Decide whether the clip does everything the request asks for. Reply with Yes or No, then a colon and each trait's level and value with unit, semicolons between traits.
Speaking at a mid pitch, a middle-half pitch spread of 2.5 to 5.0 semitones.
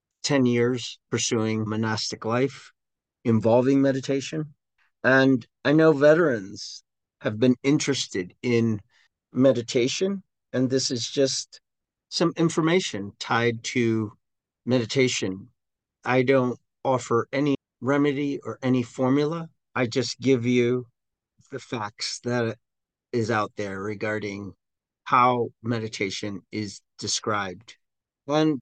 No: low, 125 Hz; average, 3.4 semitones